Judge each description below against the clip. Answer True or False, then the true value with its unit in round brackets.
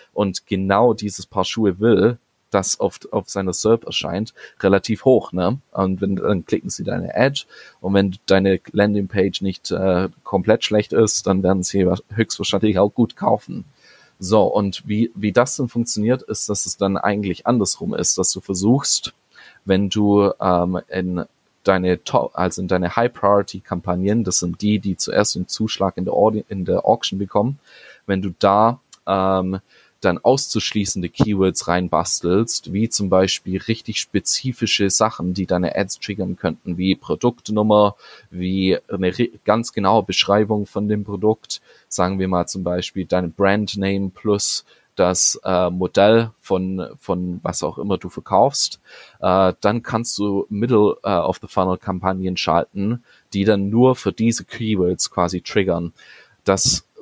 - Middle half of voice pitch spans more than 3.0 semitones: False (2.6 semitones)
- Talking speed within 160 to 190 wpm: False (150 wpm)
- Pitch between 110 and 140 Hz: False (100 Hz)